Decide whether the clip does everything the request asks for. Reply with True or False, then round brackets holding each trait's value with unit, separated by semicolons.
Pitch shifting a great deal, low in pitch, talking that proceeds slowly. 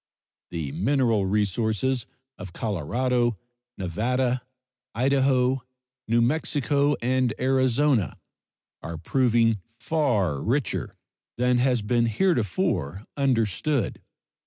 False (4.0 semitones; 120 Hz; 85 wpm)